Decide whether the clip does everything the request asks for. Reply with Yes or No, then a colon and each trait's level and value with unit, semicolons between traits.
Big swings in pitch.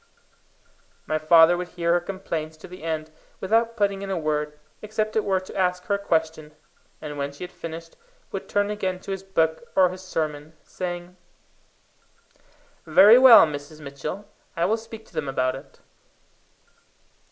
No: average, 4.0 semitones